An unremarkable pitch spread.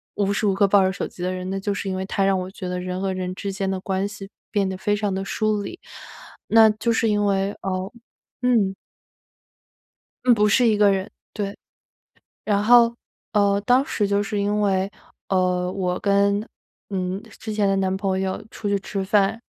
No: narrow, 1.6 semitones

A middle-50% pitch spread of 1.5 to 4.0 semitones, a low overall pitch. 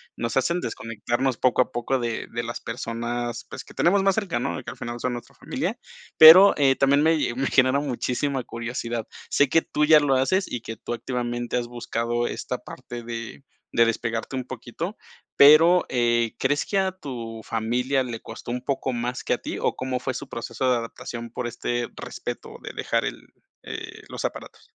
Yes: average, 2.7 semitones; low, 125 Hz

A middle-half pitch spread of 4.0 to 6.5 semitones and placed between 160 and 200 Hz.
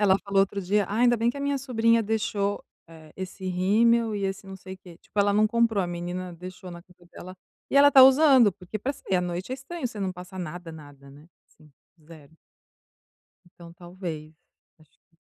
Yes: average, 4.3 semitones; high, 190 Hz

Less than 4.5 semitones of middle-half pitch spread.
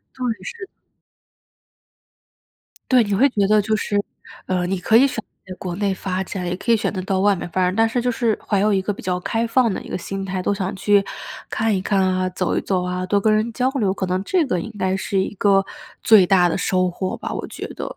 Yes: average, 2.9 semitones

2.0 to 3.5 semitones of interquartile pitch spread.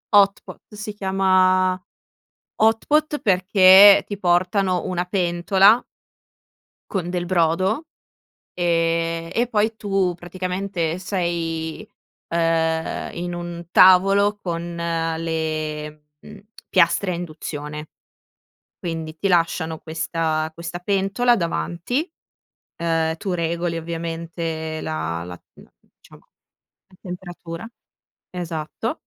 Yes: average, 2.7 semitones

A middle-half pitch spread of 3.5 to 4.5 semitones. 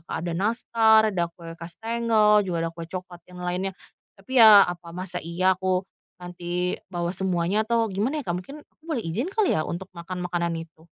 Yes: average, 4.0 semitones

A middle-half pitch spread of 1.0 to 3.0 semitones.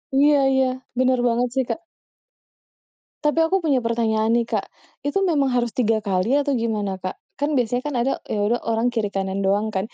No: average, 3.9 semitones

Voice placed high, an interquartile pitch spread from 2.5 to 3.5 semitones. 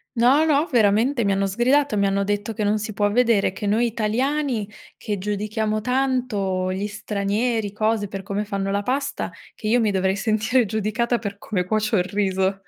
Yes: high, 210 Hz; average, 2.9 semitones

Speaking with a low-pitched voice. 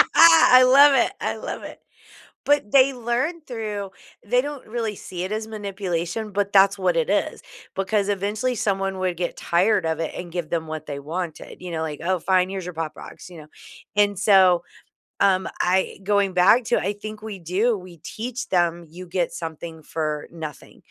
No: high, 195 Hz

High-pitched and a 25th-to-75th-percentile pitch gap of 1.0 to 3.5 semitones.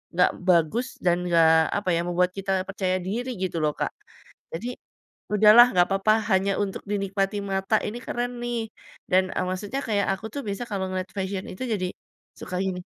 Yes: high, 195 Hz; average, 2.8 semitones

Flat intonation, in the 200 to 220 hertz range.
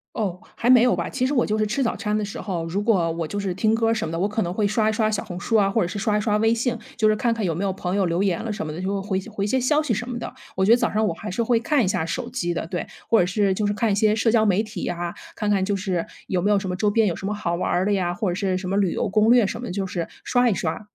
No: average, 3.3 semitones; high, 205 Hz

